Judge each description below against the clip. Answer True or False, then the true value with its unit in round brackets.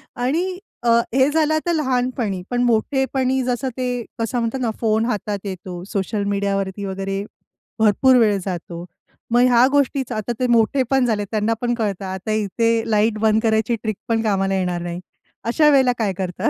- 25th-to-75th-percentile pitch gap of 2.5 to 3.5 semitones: False (4.0 semitones)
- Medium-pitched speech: False (225 Hz)